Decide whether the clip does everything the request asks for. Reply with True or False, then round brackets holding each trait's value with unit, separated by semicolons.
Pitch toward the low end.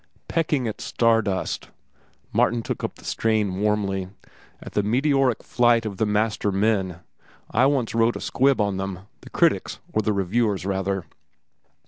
True (105 Hz)